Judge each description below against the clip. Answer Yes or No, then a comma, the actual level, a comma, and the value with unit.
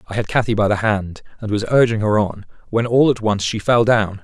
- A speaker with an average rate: No, fast, 255 wpm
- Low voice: Yes, low, 110 Hz